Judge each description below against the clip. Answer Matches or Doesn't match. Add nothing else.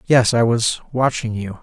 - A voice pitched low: Matches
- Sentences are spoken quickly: Doesn't match